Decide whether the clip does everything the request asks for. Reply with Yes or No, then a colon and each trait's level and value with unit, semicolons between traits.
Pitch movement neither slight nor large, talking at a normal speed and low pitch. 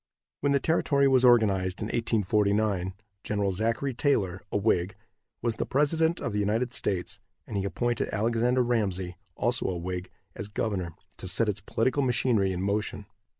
Yes: average, 4.0 semitones; average, 160 wpm; low, 105 Hz